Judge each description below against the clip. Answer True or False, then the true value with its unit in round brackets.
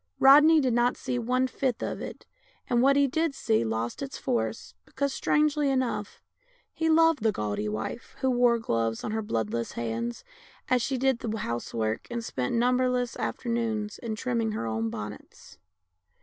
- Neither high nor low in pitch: False (235 Hz)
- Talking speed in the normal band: True (170 wpm)